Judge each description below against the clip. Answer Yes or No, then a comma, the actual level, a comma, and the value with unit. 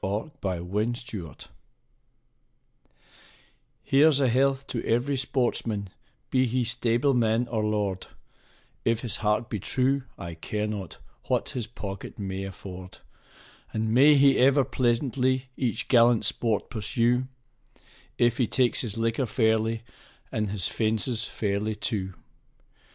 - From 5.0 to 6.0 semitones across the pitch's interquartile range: No, average, 3.3 semitones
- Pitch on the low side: Yes, low, 115 Hz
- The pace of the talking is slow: Yes, slow, 125 wpm